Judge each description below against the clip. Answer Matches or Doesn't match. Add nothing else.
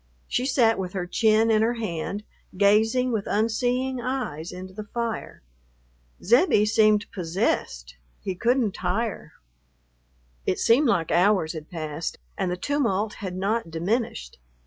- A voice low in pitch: Doesn't match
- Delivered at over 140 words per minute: Doesn't match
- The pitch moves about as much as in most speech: Matches